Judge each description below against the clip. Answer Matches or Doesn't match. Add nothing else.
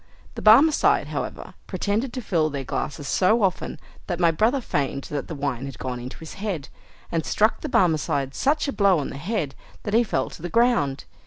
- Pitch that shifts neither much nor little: Doesn't match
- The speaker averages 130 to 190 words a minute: Doesn't match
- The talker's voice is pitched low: Doesn't match